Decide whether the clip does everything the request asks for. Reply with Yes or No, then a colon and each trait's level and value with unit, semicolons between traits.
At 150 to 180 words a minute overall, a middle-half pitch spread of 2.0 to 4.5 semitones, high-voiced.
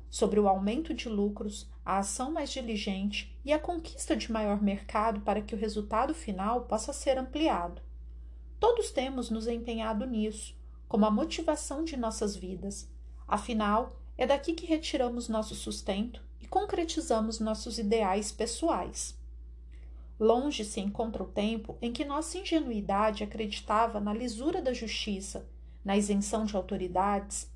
No: average, 140 wpm; average, 4.2 semitones; high, 220 Hz